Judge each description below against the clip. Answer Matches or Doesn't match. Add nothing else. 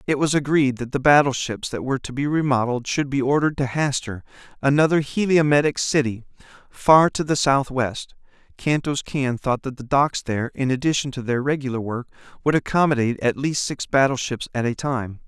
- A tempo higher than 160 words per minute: Matches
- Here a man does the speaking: Matches